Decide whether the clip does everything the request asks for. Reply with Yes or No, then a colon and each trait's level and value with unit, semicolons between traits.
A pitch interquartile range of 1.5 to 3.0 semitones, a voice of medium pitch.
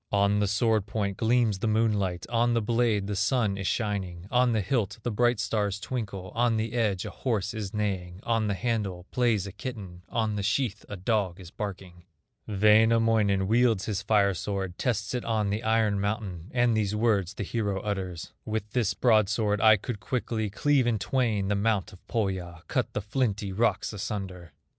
No: narrow, 2.5 semitones; low, 105 Hz